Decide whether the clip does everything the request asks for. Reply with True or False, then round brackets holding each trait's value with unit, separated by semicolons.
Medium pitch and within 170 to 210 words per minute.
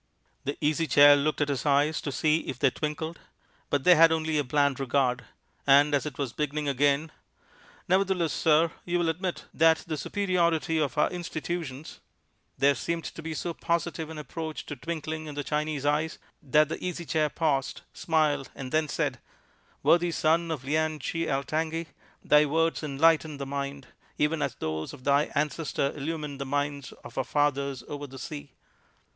True (150 Hz; 175 wpm)